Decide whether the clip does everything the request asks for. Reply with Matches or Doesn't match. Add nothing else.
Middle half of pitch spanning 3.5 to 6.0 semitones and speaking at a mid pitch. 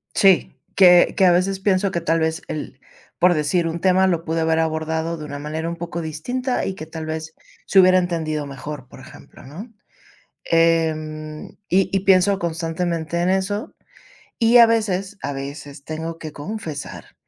Doesn't match